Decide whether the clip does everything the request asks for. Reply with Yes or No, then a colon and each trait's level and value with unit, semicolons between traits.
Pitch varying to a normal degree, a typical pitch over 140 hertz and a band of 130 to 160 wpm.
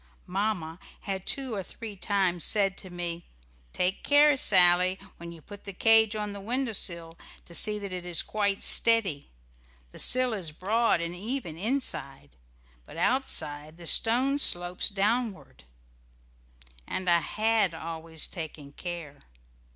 Yes: average, 4.5 semitones; high, 190 Hz; average, 145 wpm